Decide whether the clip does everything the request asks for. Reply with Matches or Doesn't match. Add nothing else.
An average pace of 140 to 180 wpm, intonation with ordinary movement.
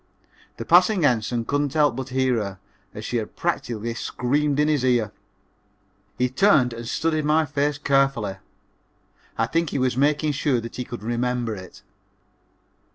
Matches